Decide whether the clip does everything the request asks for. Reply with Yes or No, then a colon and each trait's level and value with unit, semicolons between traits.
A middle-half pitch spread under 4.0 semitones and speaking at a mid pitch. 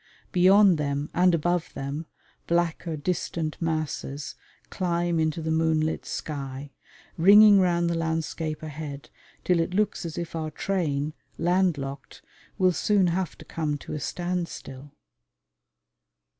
Yes: average, 2.7 semitones; medium, 165 Hz